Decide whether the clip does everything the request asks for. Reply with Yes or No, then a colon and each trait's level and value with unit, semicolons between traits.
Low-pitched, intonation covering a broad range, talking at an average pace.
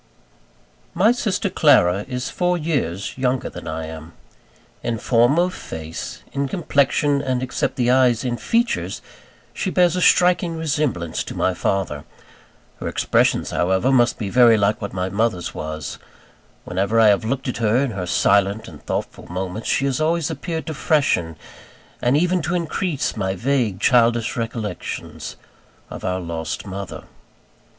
Yes: low, 120 Hz; wide, 7.6 semitones; average, 155 wpm